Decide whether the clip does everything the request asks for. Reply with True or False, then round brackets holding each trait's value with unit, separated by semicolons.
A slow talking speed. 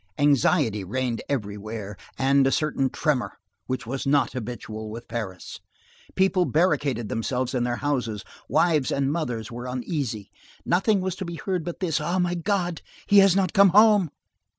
False (160 wpm)